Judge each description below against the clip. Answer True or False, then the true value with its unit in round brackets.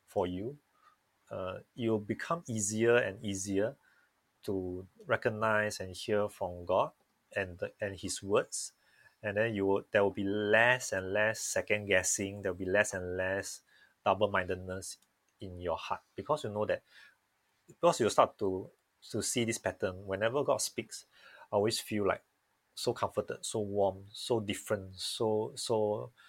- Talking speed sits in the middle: True (155 wpm)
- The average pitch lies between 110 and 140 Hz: False (100 Hz)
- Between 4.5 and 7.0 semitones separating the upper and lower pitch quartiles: False (2.6 semitones)